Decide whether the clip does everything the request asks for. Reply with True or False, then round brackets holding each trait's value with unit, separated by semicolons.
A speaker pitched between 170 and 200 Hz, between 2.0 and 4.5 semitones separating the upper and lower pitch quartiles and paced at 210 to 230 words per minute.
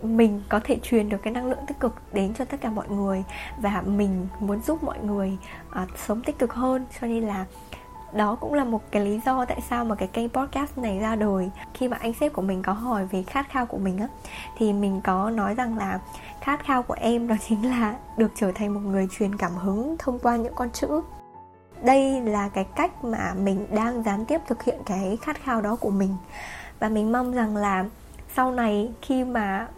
False (220 Hz; 3.9 semitones; 225 wpm)